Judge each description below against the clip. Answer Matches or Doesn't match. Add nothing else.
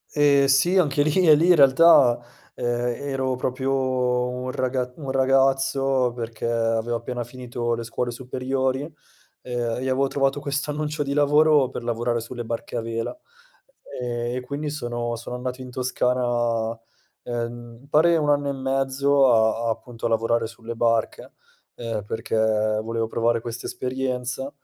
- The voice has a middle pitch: Doesn't match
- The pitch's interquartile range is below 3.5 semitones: Matches